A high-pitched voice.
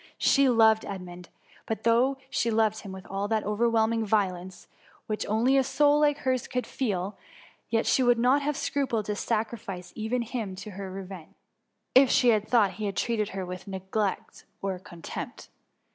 Yes: high, 220 Hz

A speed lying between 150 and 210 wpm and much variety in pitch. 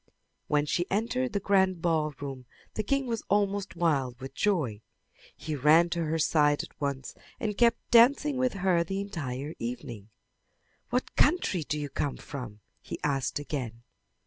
Yes: average, 160 wpm; wide, 6.4 semitones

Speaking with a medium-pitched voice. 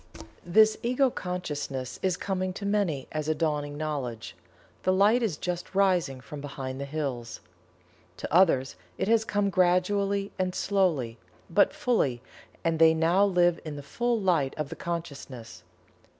Yes: medium, 170 Hz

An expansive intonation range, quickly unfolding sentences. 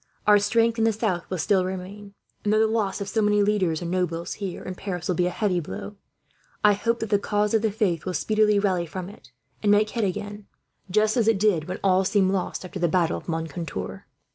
No: average, 2.7 semitones; fast, 235 wpm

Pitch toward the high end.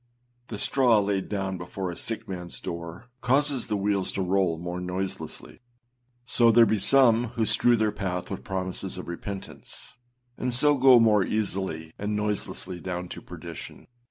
No: low, 100 Hz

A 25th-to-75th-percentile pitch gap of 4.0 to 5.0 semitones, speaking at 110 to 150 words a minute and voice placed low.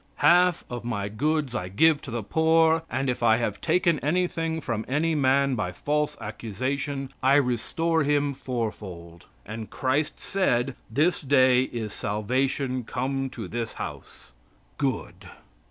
Yes: average, 4.6 semitones; average, 145 wpm; low, 130 Hz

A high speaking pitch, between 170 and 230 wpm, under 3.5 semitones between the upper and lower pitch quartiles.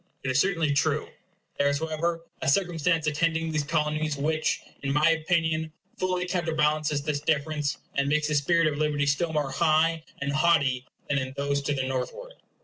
No: medium, 155 Hz; average, 175 wpm; narrow, 2.4 semitones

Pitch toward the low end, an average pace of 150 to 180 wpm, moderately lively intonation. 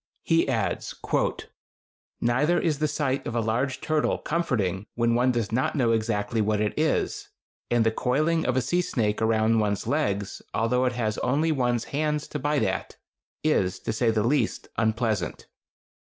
Yes: low, 120 Hz; average, 170 wpm; average, 4.8 semitones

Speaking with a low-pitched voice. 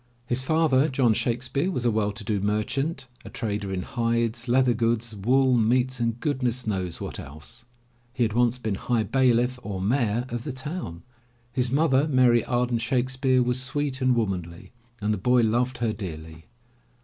Yes: low, 120 Hz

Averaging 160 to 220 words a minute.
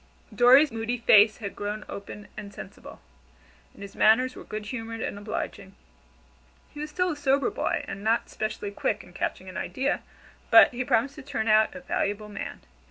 Yes: average, 180 wpm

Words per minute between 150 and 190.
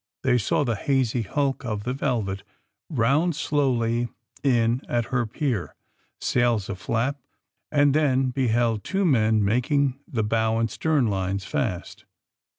No: average, 140 wpm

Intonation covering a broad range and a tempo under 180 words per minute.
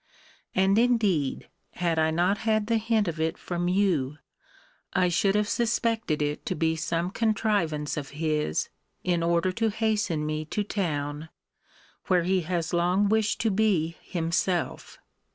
No: average, 4.7 semitones; average, 150 wpm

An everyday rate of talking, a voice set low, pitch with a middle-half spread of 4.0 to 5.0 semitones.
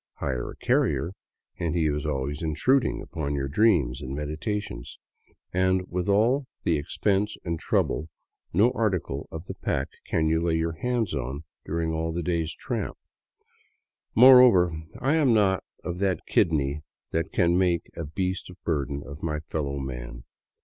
Yes: average, 155 wpm; very low, 80 Hz; average, 4.7 semitones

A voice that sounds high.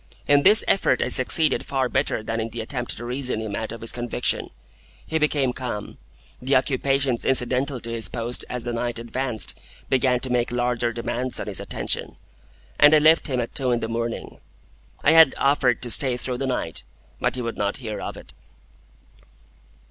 No: low, 125 Hz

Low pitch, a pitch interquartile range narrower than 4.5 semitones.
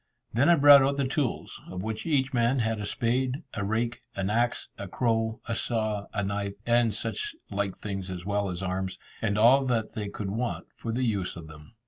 Yes: low, 110 Hz; average, 3.5 semitones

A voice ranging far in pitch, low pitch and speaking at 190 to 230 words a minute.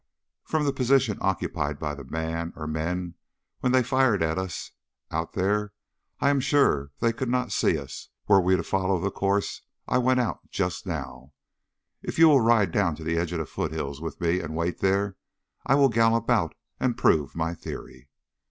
Yes: wide, 6.5 semitones; very low, 95 Hz; average, 195 wpm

